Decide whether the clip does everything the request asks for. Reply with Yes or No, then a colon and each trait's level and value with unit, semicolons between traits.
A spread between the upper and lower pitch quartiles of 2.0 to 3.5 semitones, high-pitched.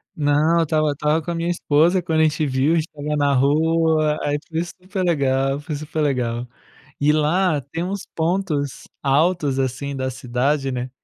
No: average, 2.9 semitones; medium, 150 Hz